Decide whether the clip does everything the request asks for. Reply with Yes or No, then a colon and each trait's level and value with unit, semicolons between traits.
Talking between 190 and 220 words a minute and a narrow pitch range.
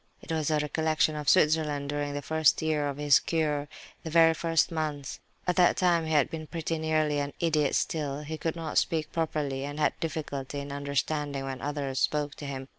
Yes: average, 200 wpm; narrow, 1.8 semitones